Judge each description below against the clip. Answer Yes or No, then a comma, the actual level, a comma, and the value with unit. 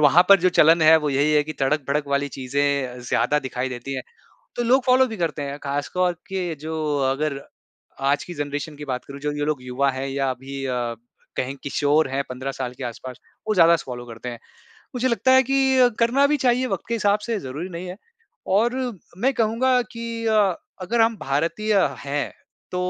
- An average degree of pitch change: No, wide, 7.8 semitones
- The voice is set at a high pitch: No, medium, 150 Hz